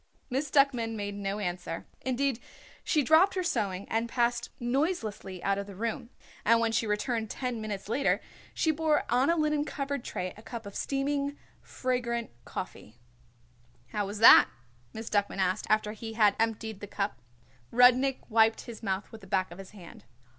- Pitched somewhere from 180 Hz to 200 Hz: No, high, 225 Hz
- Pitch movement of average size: Yes, average, 4.5 semitones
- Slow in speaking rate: No, average, 175 wpm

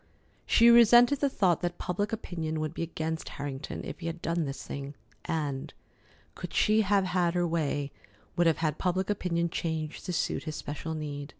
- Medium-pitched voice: Yes, medium, 170 Hz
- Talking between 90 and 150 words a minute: No, average, 185 wpm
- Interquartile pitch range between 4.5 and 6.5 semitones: No, average, 3.3 semitones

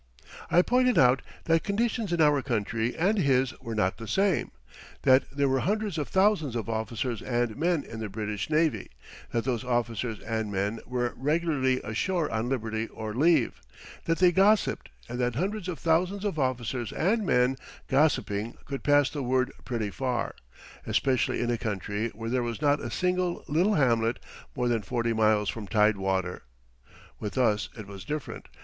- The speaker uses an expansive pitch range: Yes, wide, 6.2 semitones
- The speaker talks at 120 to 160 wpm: No, average, 175 wpm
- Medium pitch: No, low, 125 Hz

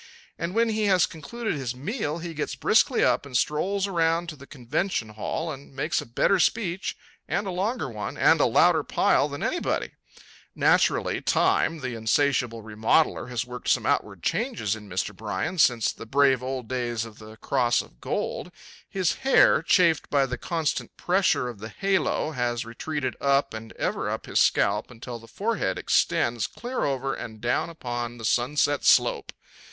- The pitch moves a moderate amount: No, wide, 6.1 semitones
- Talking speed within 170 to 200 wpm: Yes, average, 175 wpm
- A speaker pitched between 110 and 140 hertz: Yes, low, 135 Hz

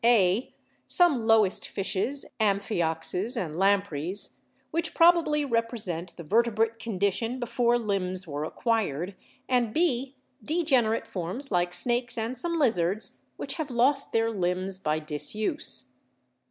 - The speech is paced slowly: Yes, slow, 125 wpm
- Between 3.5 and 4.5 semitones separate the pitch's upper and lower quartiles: No, average, 5.2 semitones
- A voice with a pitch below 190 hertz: No, high, 220 Hz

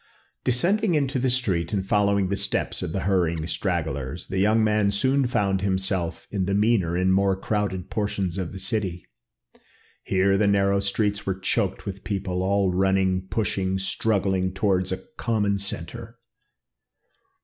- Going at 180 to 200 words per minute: No, average, 150 wpm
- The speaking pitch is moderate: No, very low, 95 Hz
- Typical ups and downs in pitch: No, narrow, 1.7 semitones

